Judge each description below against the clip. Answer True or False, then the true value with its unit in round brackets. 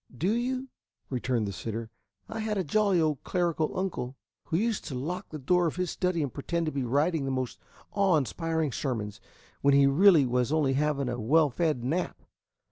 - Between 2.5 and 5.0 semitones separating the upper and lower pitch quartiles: False (5.6 semitones)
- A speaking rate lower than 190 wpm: False (195 wpm)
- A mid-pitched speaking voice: True (155 Hz)